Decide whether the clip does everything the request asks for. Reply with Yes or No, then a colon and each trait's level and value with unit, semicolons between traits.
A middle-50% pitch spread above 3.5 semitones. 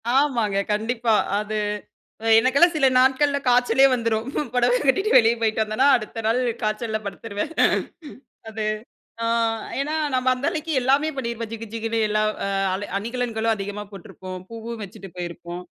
No: average, 3.2 semitones